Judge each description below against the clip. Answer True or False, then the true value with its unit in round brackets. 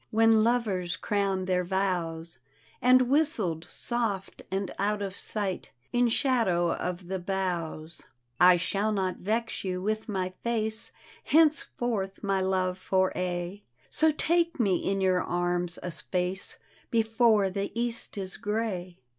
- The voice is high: True (195 Hz)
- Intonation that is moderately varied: True (3.7 semitones)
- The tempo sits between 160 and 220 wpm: False (140 wpm)